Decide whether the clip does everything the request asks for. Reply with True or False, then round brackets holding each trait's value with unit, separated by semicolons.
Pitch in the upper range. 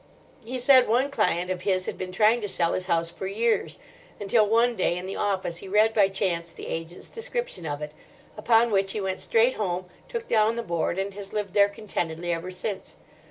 True (195 Hz)